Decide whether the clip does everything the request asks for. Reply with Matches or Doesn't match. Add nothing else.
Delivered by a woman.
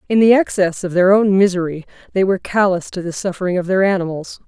Matches